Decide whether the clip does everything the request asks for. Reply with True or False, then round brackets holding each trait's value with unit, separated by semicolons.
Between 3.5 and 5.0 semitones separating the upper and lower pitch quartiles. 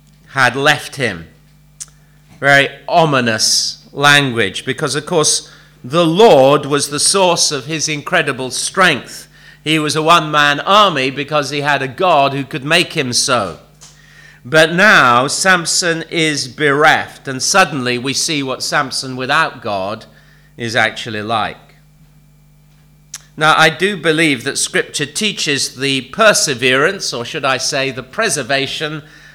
False (2.8 semitones)